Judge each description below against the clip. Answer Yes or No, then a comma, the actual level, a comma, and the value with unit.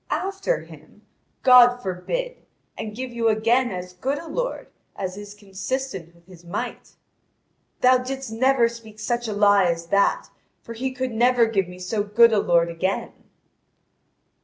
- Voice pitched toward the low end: No, high, 225 Hz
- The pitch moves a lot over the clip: No, average, 4.9 semitones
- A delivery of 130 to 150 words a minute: No, average, 160 wpm